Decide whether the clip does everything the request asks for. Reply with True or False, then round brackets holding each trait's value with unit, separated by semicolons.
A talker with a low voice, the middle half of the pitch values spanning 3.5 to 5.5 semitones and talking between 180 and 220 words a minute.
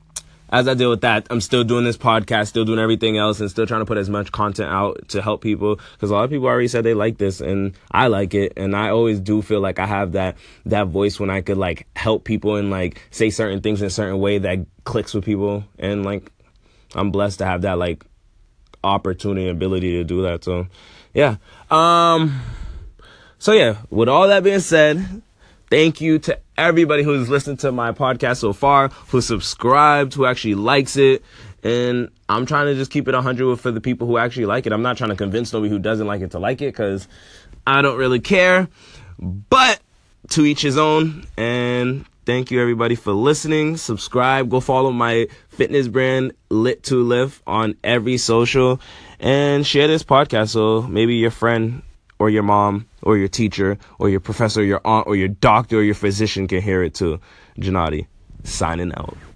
True (110 Hz; 4.1 semitones; 200 wpm)